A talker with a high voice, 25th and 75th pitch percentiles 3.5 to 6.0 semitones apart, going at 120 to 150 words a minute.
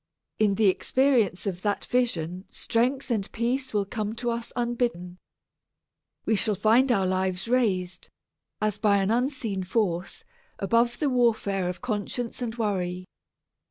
Yes: high, 215 Hz; average, 4.0 semitones; average, 140 wpm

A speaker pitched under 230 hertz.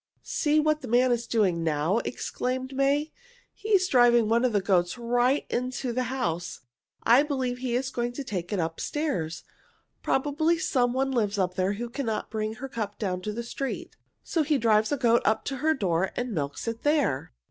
No: high, 240 Hz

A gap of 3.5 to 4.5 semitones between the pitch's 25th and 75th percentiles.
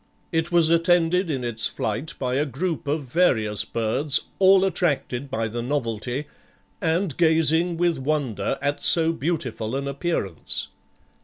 No: average, 5.0 semitones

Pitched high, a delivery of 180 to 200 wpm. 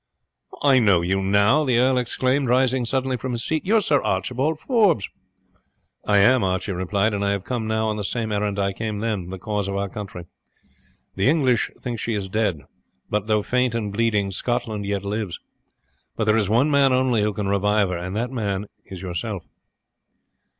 No: low, 110 Hz; average, 195 wpm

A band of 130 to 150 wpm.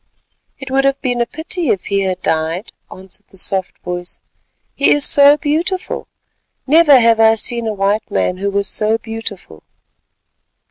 No: average, 165 wpm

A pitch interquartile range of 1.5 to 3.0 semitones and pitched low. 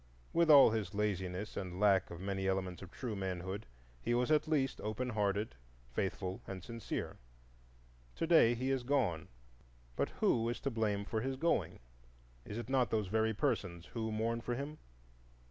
No: average, 4.4 semitones; low, 110 Hz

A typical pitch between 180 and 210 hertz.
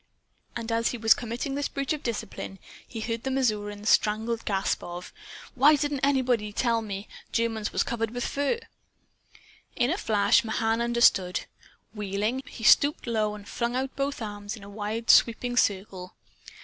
No: high, 230 Hz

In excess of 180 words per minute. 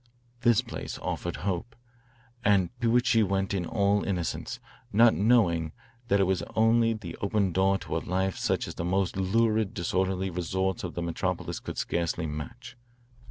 No: average, 165 wpm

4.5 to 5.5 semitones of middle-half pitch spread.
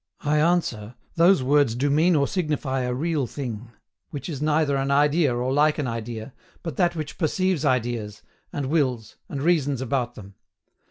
No: average, 3.8 semitones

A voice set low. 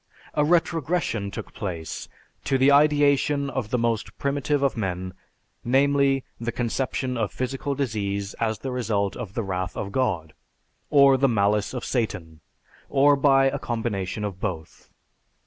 Yes: low, 120 Hz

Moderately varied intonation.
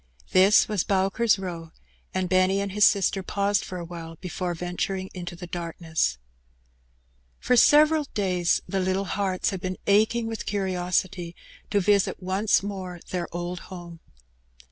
No: narrow, 2.2 semitones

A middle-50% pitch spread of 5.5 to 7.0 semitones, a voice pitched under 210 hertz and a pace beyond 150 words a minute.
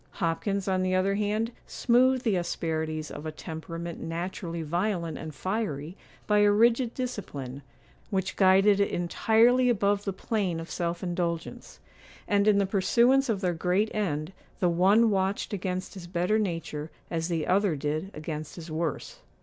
No: average, 3.8 semitones; medium, 185 Hz; average, 160 wpm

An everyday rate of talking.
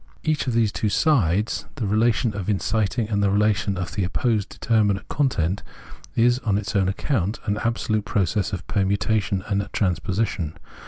Yes: average, 160 wpm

